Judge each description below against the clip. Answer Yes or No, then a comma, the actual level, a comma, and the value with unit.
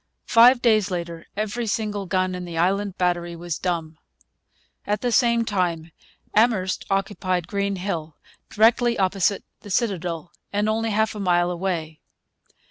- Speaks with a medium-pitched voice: No, high, 195 Hz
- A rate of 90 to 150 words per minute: Yes, average, 140 wpm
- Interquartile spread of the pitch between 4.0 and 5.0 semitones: No, average, 3.6 semitones